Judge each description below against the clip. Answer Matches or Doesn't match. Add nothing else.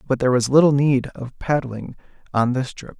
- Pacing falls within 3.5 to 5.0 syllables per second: Doesn't match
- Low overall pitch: Matches